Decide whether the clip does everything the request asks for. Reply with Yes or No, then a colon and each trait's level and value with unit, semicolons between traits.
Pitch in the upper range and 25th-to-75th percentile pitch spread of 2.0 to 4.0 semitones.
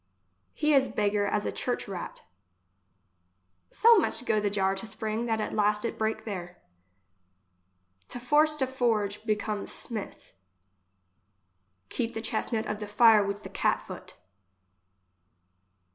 Yes: high, 215 Hz; average, 2.7 semitones